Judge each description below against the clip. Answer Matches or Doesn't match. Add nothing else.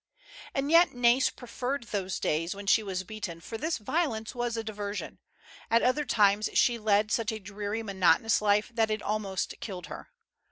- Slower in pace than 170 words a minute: Doesn't match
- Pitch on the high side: Matches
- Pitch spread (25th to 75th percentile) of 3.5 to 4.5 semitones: Doesn't match